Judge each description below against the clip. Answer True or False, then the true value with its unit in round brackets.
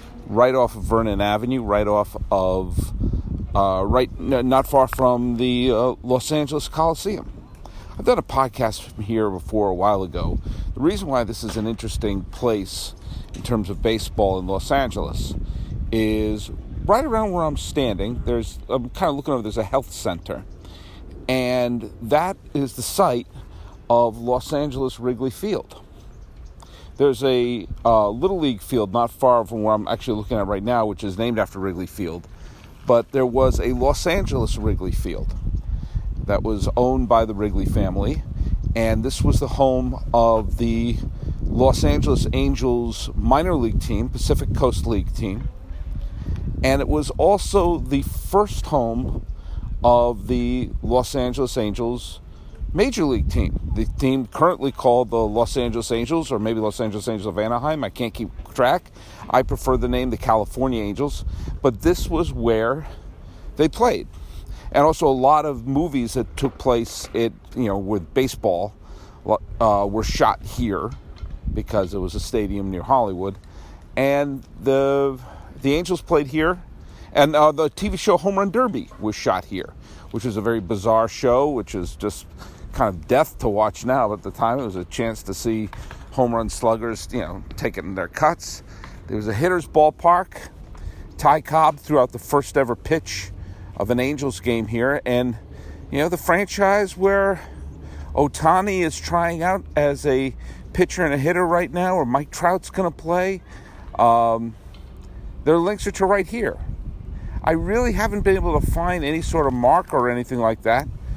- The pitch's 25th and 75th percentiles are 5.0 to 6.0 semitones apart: True (5.5 semitones)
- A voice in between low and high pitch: False (115 Hz)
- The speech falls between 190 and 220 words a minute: False (165 wpm)